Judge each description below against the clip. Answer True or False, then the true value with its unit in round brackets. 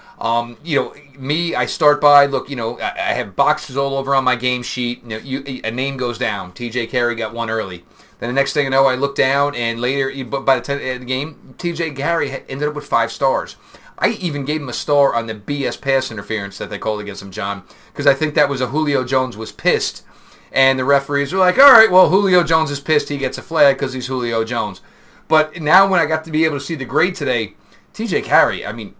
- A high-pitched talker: False (135 Hz)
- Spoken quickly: True (250 wpm)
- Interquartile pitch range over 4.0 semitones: False (3.4 semitones)